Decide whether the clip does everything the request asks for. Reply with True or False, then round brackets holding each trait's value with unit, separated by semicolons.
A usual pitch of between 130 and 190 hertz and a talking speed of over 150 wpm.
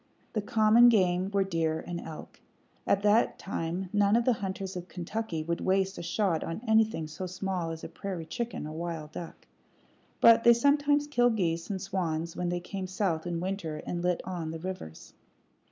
True (185 Hz; 185 wpm)